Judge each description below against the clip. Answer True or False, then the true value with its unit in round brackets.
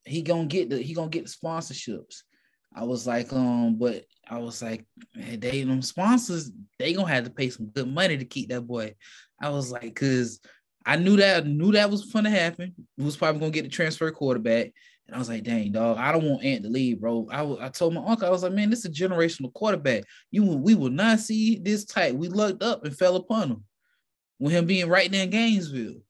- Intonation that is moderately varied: False (7.3 semitones)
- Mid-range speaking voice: True (155 Hz)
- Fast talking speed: True (230 wpm)